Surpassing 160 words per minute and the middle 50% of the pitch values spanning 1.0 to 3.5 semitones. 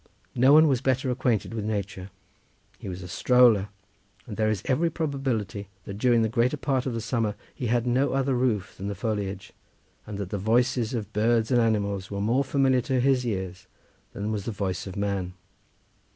No: average, 195 wpm; average, 4.1 semitones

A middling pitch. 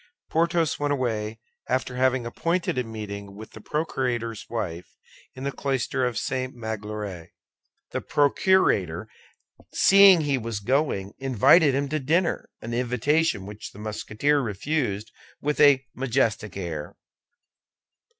No: low, 125 Hz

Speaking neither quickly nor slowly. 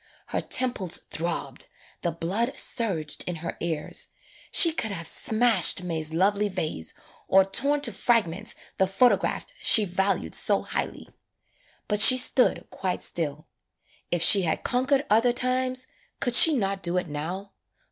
Yes: average, 145 wpm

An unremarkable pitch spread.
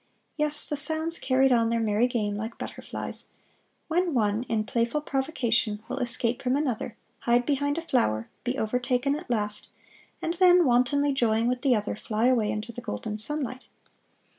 Yes: average, 4.3 semitones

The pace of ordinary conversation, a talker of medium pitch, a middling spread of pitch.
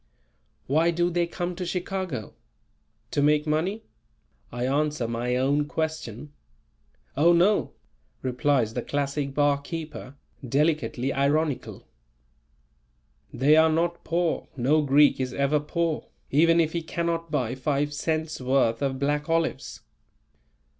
No: slow, 120 wpm; medium, 150 Hz; average, 3.2 semitones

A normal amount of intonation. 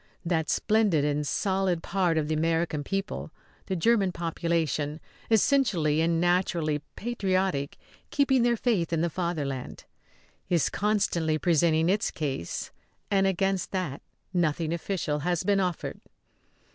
Yes: average, 3.7 semitones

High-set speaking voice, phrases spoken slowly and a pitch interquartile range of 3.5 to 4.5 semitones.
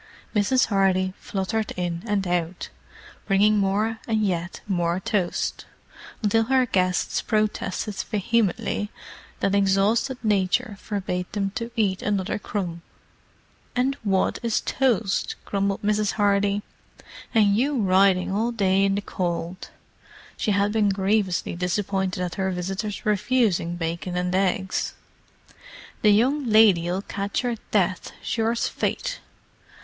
No: high, 200 Hz; slow, 125 wpm; narrow, 2.6 semitones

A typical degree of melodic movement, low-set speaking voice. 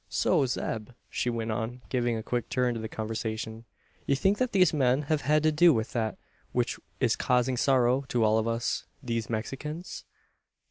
Yes: average, 3.8 semitones; low, 125 Hz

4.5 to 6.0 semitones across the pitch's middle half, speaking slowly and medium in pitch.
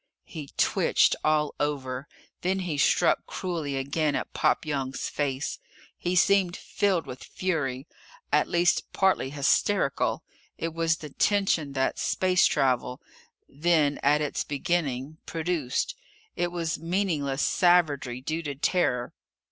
No: average, 4.1 semitones; slow, 125 wpm; medium, 155 Hz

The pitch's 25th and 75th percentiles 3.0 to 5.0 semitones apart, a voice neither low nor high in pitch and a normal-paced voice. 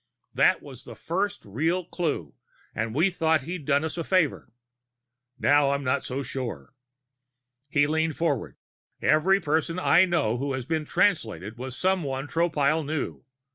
Yes: average, 4.1 semitones; medium, 150 Hz; average, 150 wpm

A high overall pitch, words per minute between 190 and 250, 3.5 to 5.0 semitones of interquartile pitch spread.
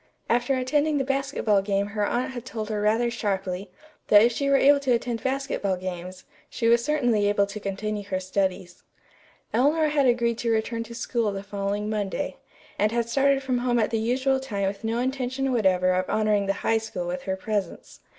Yes: high, 225 Hz; average, 200 wpm; average, 4.2 semitones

